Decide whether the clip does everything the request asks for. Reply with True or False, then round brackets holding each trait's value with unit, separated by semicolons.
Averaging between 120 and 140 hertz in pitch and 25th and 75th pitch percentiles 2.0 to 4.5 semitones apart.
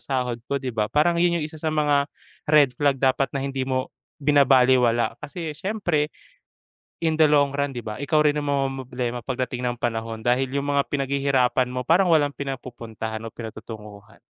True (135 Hz; 3.1 semitones)